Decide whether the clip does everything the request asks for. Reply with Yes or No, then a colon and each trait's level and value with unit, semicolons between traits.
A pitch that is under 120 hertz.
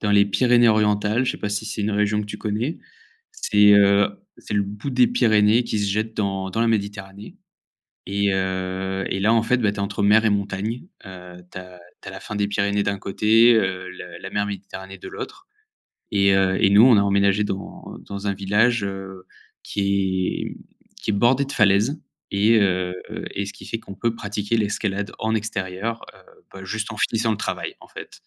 Yes: low, 100 Hz